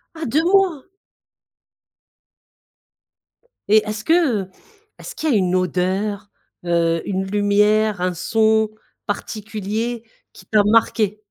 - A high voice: Yes, high, 210 Hz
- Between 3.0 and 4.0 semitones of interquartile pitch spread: No, narrow, 2.6 semitones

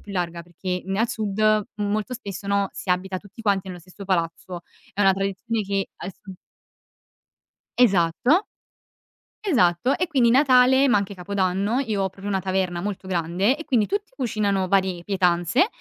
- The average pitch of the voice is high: Yes, high, 195 Hz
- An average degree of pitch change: Yes, average, 3.7 semitones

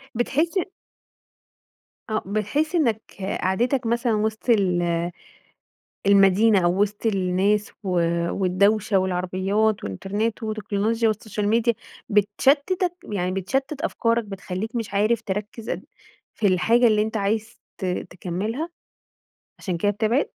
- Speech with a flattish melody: No, average, 3.1 semitones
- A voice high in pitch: Yes, high, 210 Hz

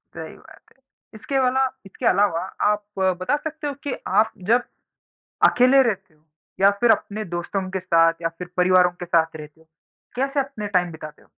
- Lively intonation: Yes, wide, 6.5 semitones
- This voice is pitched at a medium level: No, high, 195 Hz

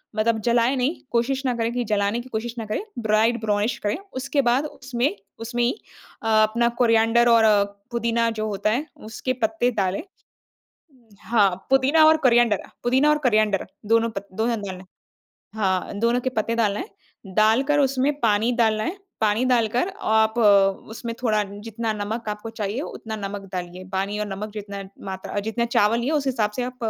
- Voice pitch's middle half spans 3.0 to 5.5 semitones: No, narrow, 2.6 semitones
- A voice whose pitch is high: Yes, high, 230 Hz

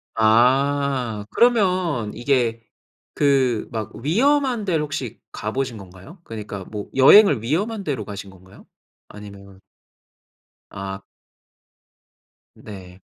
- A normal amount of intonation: No, wide, 6.5 semitones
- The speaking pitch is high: No, low, 120 Hz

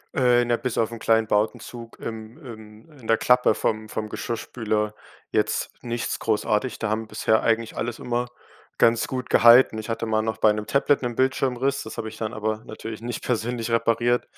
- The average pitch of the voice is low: Yes, low, 115 Hz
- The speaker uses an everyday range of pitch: No, narrow, 1.8 semitones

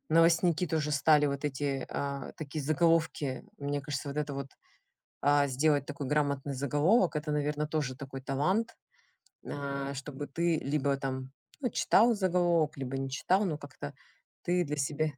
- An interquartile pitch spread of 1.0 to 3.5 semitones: Yes, narrow, 2.4 semitones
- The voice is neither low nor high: Yes, medium, 145 Hz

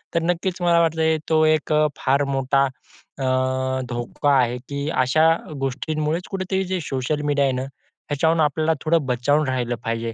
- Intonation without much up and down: No, average, 3.5 semitones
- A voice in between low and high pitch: Yes, medium, 145 Hz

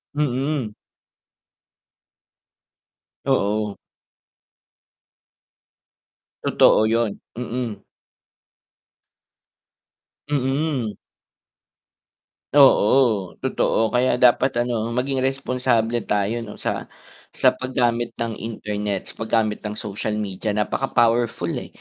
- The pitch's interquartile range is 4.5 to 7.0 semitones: No, average, 3.2 semitones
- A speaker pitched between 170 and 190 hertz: No, low, 115 Hz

